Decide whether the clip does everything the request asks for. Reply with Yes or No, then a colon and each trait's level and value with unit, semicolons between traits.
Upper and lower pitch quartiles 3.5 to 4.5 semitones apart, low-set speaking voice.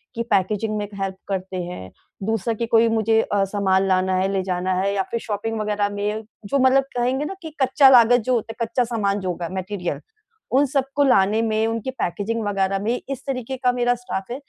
No: average, 3.9 semitones; high, 220 Hz